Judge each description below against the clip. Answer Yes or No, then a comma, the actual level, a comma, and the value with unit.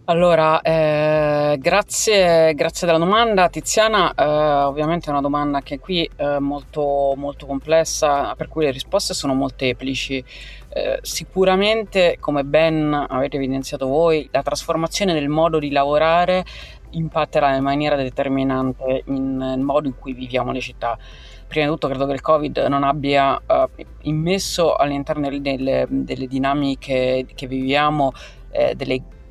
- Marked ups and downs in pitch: No, average, 3.2 semitones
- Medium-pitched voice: Yes, medium, 145 Hz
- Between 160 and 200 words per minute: No, average, 140 wpm